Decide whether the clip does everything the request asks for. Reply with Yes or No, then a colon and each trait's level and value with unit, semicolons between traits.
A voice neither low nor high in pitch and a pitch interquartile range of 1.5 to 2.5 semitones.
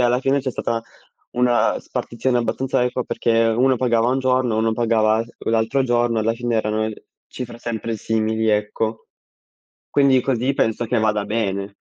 No: low, 115 Hz; narrow, 2.0 semitones